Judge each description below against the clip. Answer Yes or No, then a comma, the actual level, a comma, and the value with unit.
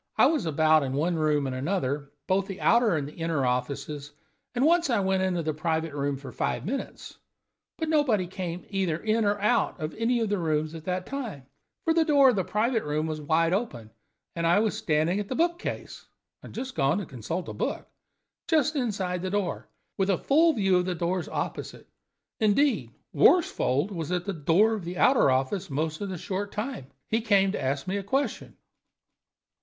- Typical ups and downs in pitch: No, wide, 5.9 semitones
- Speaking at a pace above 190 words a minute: Yes, fast, 205 wpm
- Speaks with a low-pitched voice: No, medium, 185 Hz